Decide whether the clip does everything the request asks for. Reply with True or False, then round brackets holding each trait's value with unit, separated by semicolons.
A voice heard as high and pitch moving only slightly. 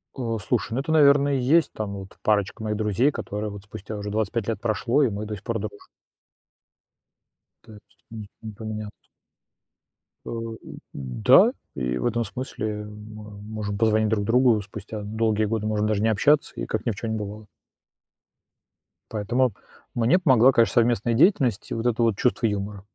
False (110 Hz; 2.2 semitones)